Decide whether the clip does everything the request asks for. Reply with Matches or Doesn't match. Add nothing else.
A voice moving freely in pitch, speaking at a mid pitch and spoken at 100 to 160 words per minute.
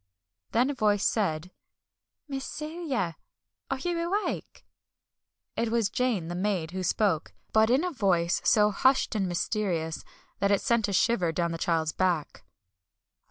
Doesn't match